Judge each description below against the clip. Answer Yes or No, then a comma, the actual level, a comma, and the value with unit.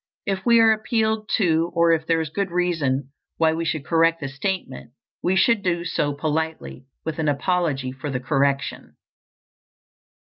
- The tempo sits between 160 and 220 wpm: Yes, average, 165 wpm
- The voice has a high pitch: No, medium, 165 Hz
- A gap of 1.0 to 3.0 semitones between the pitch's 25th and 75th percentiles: No, average, 4.1 semitones